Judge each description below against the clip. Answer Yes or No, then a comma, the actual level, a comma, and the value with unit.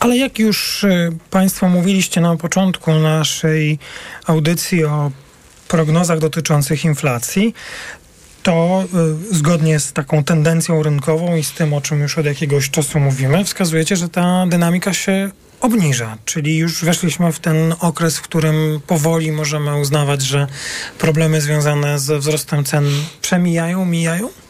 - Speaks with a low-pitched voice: No, medium, 160 Hz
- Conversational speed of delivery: Yes, average, 130 wpm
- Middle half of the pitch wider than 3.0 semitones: No, narrow, 2.4 semitones